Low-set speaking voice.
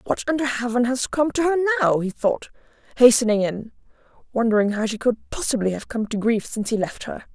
No: high, 240 Hz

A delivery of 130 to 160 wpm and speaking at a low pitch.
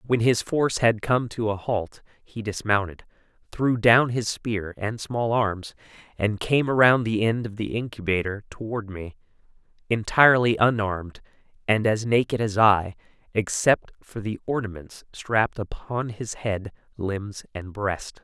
Yes: average, 150 wpm; low, 110 Hz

